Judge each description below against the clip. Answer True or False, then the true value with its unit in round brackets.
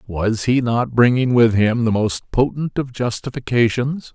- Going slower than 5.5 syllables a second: True (4.2 syllables/s)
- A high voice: False (120 Hz)